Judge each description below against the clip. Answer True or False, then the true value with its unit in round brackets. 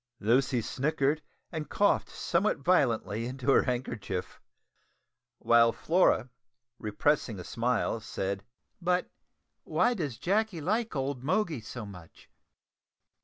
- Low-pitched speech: True (130 Hz)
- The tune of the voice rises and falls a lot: True (6.5 semitones)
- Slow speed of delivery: True (110 wpm)